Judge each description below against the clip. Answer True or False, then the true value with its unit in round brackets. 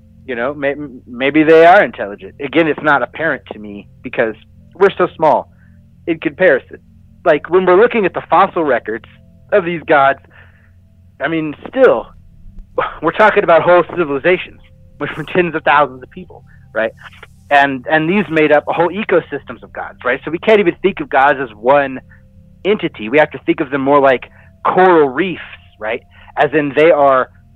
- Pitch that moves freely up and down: True (7.5 semitones)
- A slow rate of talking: False (175 wpm)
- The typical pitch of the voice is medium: True (145 Hz)